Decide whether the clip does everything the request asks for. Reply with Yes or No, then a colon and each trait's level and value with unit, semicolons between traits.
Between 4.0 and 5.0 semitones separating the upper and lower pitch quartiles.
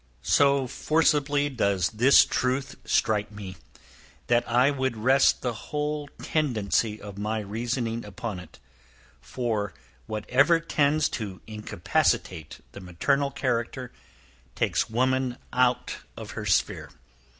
Yes: average, 4.5 semitones